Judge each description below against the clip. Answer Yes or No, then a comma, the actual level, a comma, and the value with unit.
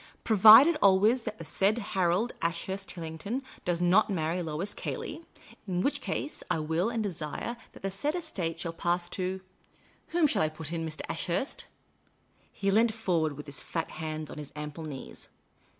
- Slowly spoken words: No, average, 175 wpm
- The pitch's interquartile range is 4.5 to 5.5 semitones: Yes, average, 5.1 semitones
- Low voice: No, medium, 180 Hz